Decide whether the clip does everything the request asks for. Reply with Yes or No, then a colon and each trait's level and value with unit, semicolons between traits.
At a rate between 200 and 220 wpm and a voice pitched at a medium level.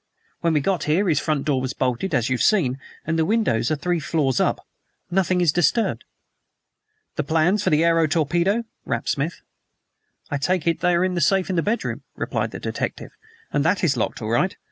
Yes: fast, 205 wpm; medium, 165 Hz